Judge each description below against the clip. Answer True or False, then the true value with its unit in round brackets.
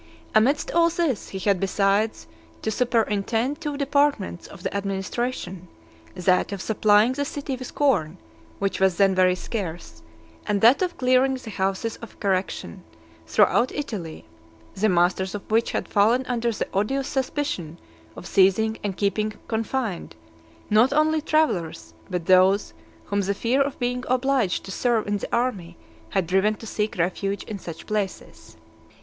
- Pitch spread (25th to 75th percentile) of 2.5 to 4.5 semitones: False (4.9 semitones)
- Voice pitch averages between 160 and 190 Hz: False (210 Hz)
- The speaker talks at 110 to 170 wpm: True (155 wpm)